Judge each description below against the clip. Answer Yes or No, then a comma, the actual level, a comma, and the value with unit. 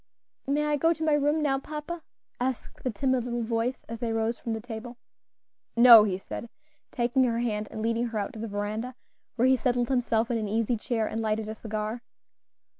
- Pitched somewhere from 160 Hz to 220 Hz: No, high, 235 Hz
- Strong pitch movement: No, average, 2.7 semitones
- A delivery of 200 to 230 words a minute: Yes, fast, 205 wpm